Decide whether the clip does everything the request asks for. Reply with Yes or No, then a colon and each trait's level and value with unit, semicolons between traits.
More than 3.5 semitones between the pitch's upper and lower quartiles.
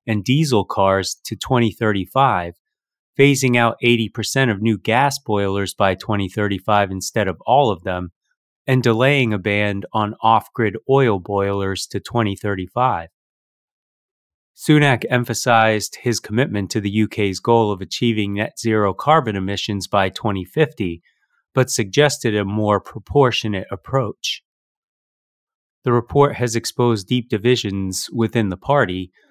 Yes: average, 3.9 semitones